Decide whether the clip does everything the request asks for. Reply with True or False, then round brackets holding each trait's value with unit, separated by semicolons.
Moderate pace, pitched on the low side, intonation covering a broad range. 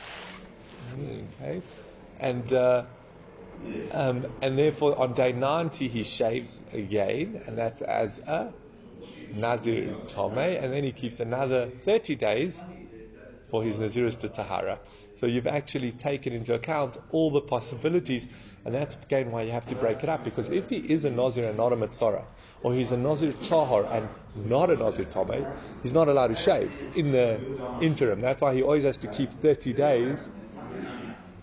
False (165 wpm; 130 Hz; 3.3 semitones)